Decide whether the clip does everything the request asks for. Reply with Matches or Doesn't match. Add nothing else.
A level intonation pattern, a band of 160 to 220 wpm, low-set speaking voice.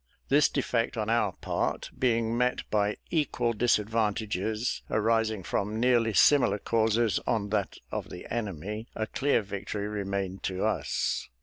Doesn't match